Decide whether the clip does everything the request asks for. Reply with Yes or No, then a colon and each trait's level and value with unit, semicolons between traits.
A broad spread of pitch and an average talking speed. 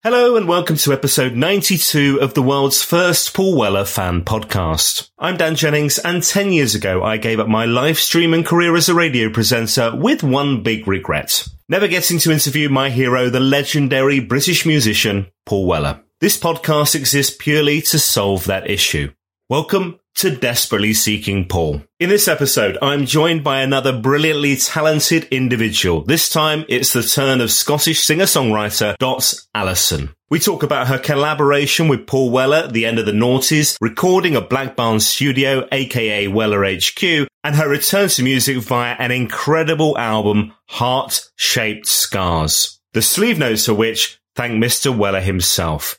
Yes: wide, 6.0 semitones; average, 165 wpm